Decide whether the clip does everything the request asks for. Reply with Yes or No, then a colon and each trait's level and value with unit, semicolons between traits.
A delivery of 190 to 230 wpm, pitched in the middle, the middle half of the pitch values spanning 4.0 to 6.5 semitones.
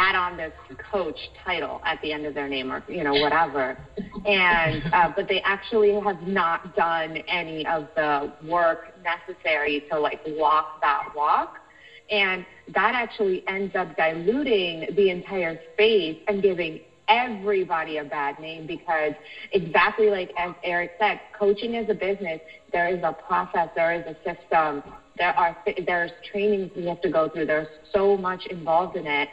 No: average, 165 wpm; medium, 180 Hz; average, 4.4 semitones